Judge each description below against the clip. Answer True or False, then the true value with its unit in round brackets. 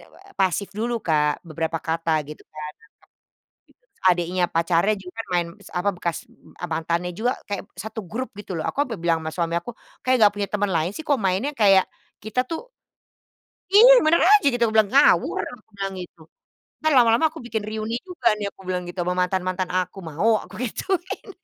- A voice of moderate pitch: False (195 Hz)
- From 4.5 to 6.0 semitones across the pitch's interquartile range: True (5.6 semitones)